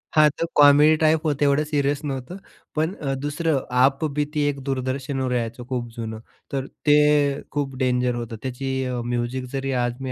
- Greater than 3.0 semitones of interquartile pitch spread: No, narrow, 2.6 semitones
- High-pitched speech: No, low, 135 Hz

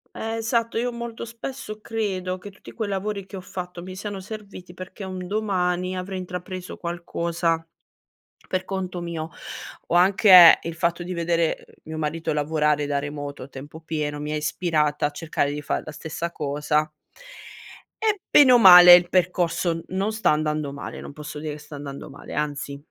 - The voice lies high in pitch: No, medium, 175 Hz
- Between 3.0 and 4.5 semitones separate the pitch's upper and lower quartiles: Yes, average, 3.9 semitones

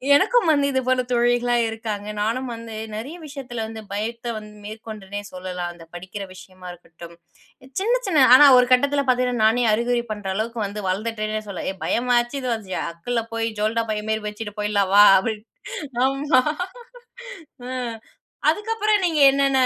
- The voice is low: No, high, 230 Hz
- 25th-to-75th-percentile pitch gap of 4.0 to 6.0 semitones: No, average, 3.5 semitones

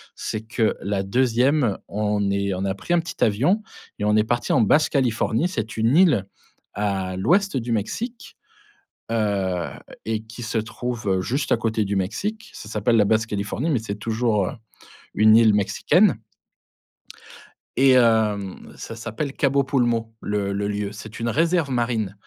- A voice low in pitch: Yes, low, 110 Hz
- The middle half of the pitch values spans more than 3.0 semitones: Yes, average, 3.5 semitones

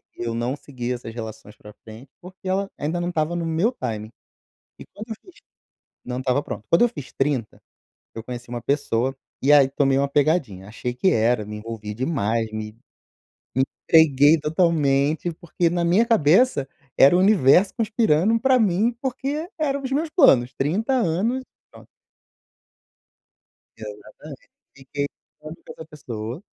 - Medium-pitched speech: Yes, medium, 150 Hz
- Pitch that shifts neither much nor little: No, wide, 7.7 semitones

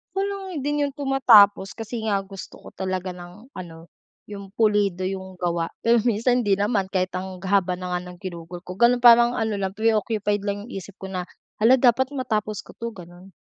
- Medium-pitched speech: No, high, 205 Hz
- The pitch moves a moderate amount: Yes, average, 4.2 semitones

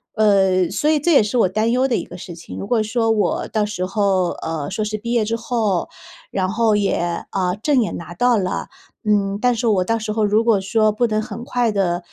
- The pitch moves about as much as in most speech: Yes, average, 3.1 semitones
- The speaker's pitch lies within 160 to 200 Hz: No, high, 215 Hz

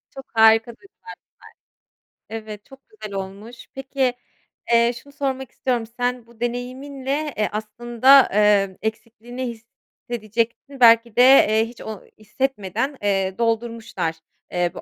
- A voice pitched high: Yes, high, 235 Hz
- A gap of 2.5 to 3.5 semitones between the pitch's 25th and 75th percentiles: Yes, average, 3.2 semitones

